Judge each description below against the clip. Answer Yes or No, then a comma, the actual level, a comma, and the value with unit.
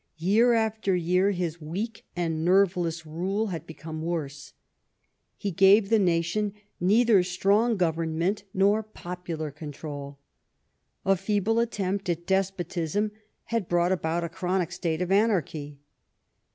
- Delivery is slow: Yes, slow, 125 wpm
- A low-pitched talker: No, medium, 180 Hz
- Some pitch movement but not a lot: Yes, average, 3.5 semitones